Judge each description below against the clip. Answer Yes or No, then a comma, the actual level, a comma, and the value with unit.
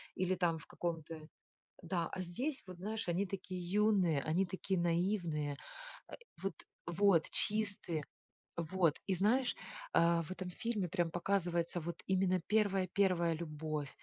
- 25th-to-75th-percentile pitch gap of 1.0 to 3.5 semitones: Yes, narrow, 2.6 semitones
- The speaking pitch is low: No, medium, 180 Hz